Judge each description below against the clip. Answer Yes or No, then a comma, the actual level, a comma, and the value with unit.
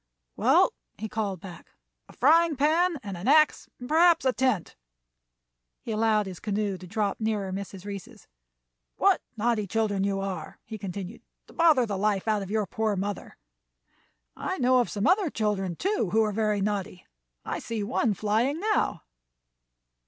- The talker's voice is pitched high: Yes, high, 215 Hz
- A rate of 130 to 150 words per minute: No, average, 165 wpm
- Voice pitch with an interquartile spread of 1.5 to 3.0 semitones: No, average, 4.2 semitones